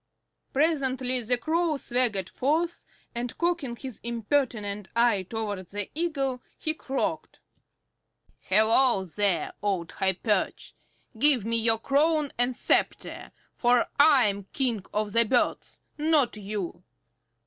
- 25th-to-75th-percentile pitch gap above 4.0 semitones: Yes, average, 5.2 semitones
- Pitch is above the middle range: Yes, high, 240 Hz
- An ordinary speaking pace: No, slow, 120 wpm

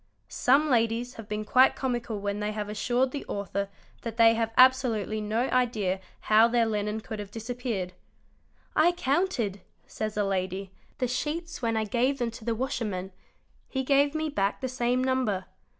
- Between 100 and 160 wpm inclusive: No, average, 175 wpm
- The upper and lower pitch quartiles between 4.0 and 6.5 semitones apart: No, average, 3.6 semitones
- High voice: Yes, high, 230 Hz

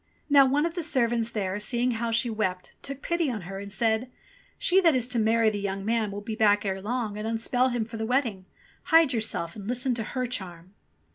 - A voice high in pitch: Yes, high, 225 Hz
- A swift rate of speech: Yes, fast, 230 wpm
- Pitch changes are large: No, average, 3.6 semitones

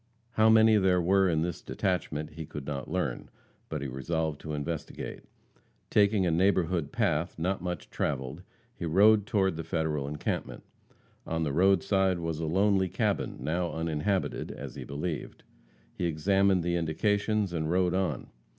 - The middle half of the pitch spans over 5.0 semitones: No, average, 3.6 semitones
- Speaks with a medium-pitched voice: No, very low, 85 Hz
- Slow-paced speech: No, average, 155 wpm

